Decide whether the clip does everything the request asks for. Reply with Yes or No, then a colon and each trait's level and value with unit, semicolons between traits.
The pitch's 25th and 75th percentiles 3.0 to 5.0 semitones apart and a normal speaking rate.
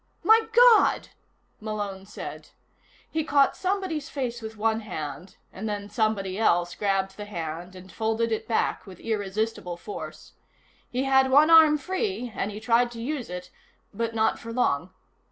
No: wide, 5.5 semitones; average, 155 wpm